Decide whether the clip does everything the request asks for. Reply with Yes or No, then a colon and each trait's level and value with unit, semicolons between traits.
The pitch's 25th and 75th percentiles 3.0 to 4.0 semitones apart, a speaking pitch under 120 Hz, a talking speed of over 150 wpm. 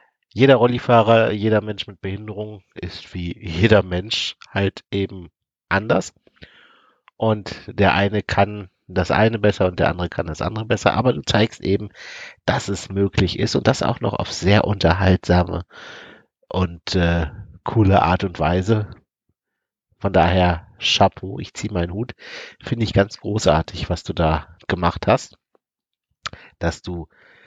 No: average, 3.3 semitones; low, 100 Hz; average, 145 wpm